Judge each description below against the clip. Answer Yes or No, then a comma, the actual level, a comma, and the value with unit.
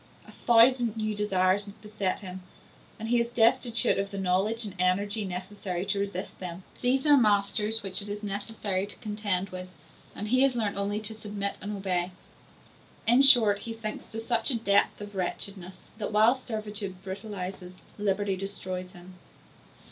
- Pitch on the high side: Yes, high, 205 Hz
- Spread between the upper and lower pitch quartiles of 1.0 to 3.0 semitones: Yes, average, 2.7 semitones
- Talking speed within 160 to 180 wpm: Yes, average, 165 wpm